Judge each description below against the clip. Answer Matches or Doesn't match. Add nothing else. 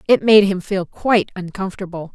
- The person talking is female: Matches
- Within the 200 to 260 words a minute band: Doesn't match